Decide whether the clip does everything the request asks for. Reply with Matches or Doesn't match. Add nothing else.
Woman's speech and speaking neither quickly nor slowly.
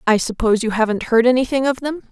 Doesn't match